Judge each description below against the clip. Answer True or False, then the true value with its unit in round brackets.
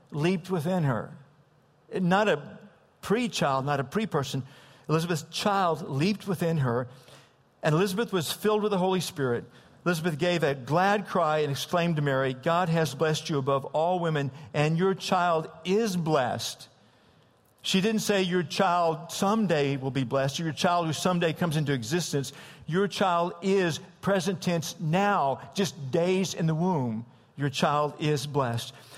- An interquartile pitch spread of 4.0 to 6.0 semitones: True (4.4 semitones)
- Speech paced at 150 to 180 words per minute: True (160 wpm)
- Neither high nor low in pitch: True (165 Hz)